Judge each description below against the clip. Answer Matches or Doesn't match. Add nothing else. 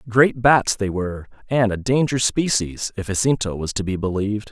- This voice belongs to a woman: Doesn't match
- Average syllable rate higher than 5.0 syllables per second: Matches